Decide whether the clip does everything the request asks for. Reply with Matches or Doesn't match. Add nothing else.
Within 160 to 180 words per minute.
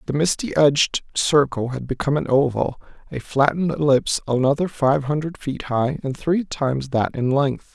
Matches